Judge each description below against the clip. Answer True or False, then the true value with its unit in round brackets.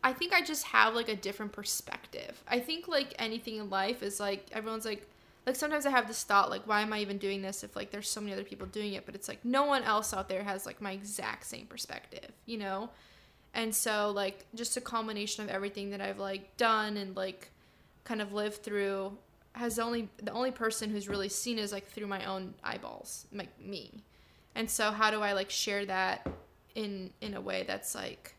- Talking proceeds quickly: True (220 wpm)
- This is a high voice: True (210 Hz)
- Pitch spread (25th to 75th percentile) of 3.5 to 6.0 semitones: False (2.5 semitones)